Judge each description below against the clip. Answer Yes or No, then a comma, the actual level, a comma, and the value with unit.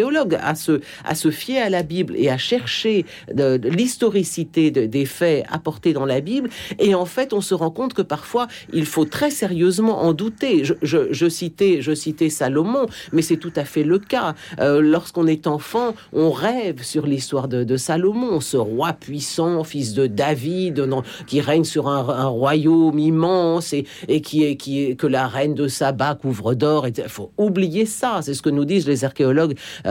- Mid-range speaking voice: Yes, medium, 160 Hz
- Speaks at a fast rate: No, average, 200 wpm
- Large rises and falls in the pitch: No, average, 4.5 semitones